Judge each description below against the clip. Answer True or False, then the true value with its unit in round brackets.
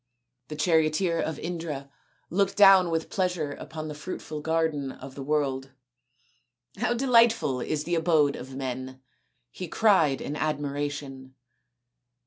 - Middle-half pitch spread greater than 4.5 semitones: False (3.9 semitones)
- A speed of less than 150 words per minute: True (140 wpm)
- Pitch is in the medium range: True (150 Hz)